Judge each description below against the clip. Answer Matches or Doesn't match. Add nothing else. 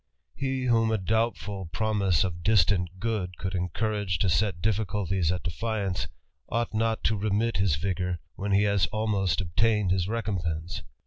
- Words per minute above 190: Doesn't match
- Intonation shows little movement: Doesn't match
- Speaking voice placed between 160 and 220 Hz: Doesn't match